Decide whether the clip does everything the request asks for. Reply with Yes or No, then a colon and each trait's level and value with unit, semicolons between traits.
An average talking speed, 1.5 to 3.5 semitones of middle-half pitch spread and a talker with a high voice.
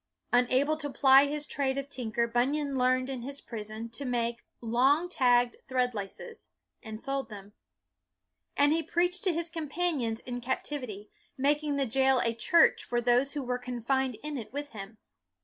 Yes: average, 175 wpm; average, 3.2 semitones; very high, 260 Hz